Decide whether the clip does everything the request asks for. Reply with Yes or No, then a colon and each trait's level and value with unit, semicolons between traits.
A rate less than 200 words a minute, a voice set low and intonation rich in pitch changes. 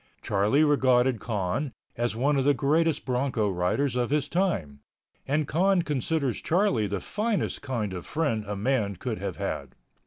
Yes: average, 160 wpm; low, 130 Hz; wide, 5.8 semitones